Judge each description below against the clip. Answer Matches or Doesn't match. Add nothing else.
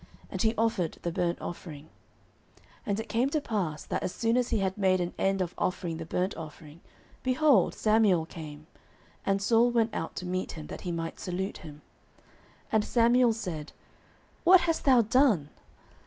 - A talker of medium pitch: Doesn't match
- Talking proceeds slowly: Doesn't match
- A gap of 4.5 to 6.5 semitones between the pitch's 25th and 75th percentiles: Matches